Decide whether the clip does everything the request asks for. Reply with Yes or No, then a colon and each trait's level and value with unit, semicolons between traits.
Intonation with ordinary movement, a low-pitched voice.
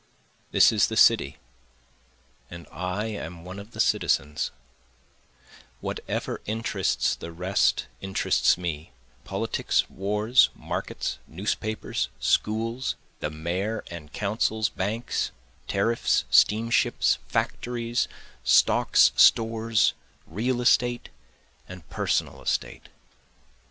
Yes: average, 4.4 semitones; low, 105 Hz